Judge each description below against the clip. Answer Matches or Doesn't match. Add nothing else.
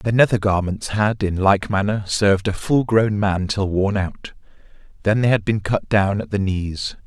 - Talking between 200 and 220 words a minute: Matches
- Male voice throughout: Matches